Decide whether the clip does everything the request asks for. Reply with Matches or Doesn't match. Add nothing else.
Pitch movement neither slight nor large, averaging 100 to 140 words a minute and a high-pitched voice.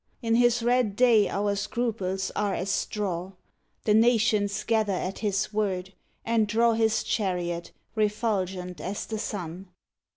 Matches